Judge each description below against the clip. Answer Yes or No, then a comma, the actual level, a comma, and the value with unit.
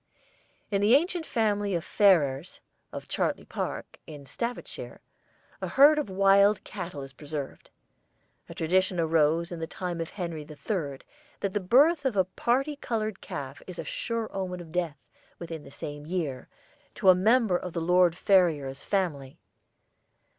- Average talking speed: Yes, average, 155 wpm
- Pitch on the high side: No, medium, 180 Hz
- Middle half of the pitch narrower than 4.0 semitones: No, average, 4.7 semitones